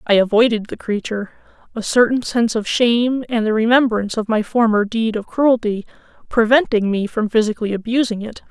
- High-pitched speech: Yes, high, 225 Hz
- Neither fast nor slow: Yes, average, 170 wpm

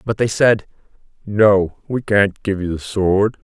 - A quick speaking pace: No, average, 170 wpm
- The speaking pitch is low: Yes, low, 100 Hz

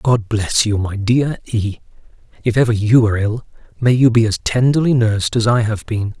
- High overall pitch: No, low, 115 Hz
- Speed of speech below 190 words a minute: No, fast, 205 wpm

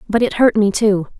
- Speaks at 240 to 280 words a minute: Yes, fast, 250 wpm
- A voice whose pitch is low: No, high, 210 Hz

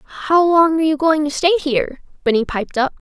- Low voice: No, very high, 300 Hz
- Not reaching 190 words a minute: No, average, 195 wpm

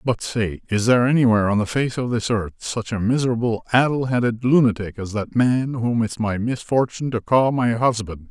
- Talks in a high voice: No, low, 115 Hz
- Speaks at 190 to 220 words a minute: Yes, average, 200 wpm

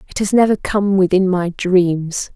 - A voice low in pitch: No, medium, 185 Hz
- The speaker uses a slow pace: No, average, 180 wpm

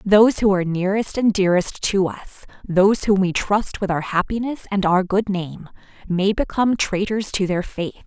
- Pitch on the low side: No, high, 195 Hz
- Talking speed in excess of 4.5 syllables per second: Yes, 5.4 syllables/s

